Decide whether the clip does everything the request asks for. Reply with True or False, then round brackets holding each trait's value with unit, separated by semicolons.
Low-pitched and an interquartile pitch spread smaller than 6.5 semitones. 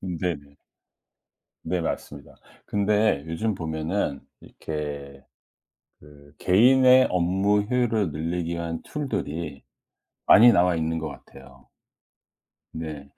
True (85 Hz; 5.5 semitones)